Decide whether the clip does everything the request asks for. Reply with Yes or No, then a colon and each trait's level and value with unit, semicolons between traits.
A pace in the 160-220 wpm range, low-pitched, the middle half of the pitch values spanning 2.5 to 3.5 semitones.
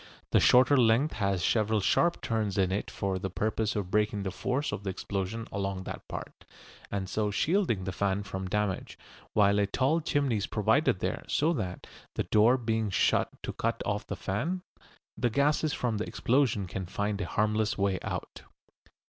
No: average, 180 wpm; low, 105 Hz; average, 3.9 semitones